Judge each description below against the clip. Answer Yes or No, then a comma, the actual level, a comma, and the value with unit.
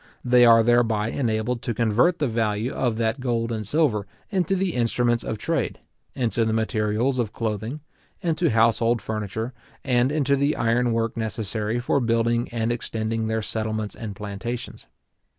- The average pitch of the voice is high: No, low, 115 Hz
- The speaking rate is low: No, average, 155 wpm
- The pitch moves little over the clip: Yes, narrow, 2.1 semitones